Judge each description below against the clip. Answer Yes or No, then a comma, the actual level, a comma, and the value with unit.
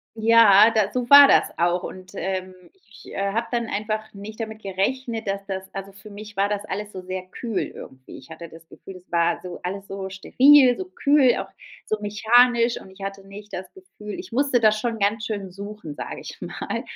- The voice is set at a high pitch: Yes, high, 205 Hz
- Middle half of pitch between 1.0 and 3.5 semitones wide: Yes, average, 3.1 semitones